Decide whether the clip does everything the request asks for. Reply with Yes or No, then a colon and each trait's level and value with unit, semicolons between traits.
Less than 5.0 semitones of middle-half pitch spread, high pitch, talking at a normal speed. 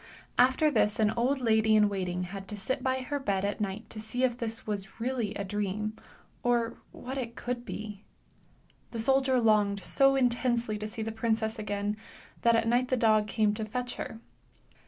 Yes: average, 2.8 semitones; high, 220 Hz; average, 190 wpm